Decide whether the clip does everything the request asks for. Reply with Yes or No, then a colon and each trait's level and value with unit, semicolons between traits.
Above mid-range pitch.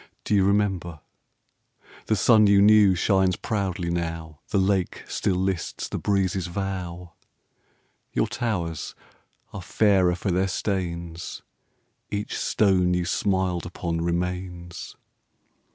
No: very low, 95 Hz